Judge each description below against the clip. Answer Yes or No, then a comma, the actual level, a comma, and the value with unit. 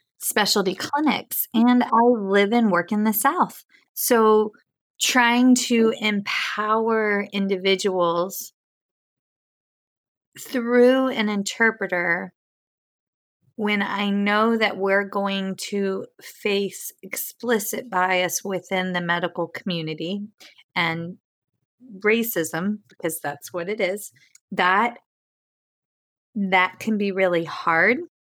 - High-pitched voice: Yes, high, 205 Hz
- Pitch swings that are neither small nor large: Yes, average, 3.4 semitones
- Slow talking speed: Yes, slow, 95 wpm